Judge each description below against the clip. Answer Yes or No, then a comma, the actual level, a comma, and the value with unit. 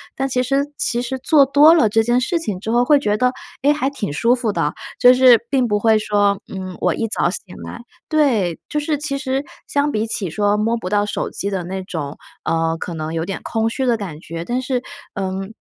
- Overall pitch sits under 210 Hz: No, high, 225 Hz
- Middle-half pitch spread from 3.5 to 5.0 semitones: No, wide, 5.4 semitones